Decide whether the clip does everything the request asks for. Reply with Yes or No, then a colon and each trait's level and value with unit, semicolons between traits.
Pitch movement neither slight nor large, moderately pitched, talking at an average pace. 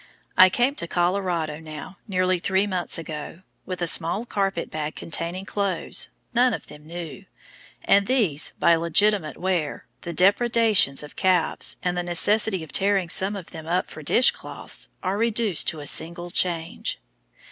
Yes: average, 3.3 semitones; medium, 180 Hz; average, 160 wpm